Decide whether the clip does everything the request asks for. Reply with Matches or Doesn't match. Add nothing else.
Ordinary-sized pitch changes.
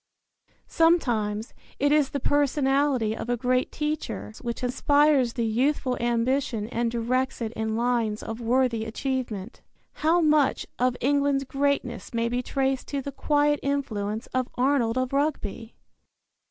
Matches